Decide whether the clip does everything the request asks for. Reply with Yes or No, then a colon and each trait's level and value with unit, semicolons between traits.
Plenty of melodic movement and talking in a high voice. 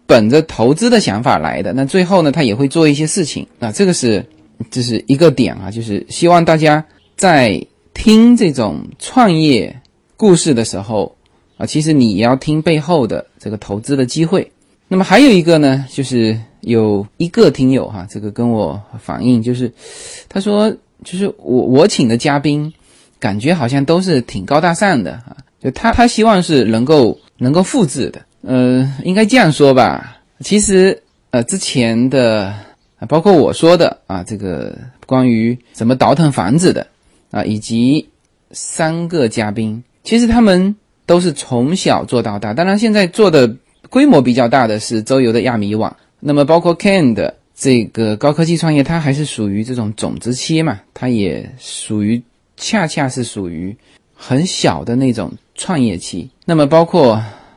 No: wide, 7.0 semitones; low, 135 Hz